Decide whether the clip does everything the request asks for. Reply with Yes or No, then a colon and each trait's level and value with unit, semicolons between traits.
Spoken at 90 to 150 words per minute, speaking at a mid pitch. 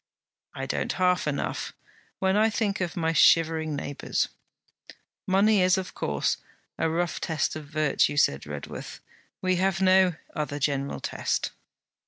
Yes: average, 140 wpm; medium, 165 Hz